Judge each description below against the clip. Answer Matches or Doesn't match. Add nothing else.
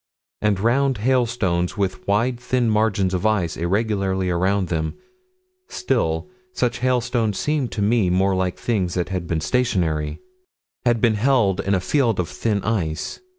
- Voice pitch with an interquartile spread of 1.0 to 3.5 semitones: Doesn't match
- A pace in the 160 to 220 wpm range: Doesn't match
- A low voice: Matches